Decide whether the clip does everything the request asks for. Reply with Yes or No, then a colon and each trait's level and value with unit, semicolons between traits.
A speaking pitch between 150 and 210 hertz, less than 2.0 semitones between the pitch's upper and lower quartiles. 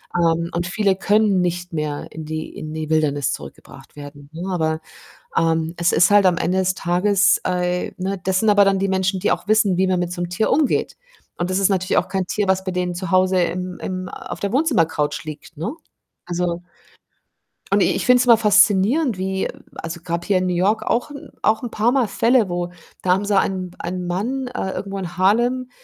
No: medium, 185 Hz; average, 2.7 semitones